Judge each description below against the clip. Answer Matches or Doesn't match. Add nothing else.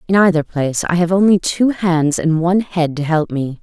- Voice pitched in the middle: Matches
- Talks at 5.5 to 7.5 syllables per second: Doesn't match